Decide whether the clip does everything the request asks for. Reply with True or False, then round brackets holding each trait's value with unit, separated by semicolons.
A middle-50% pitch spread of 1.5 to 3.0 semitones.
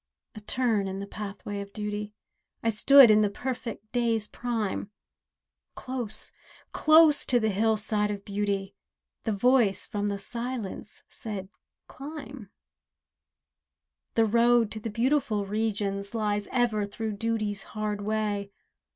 True (2.4 semitones)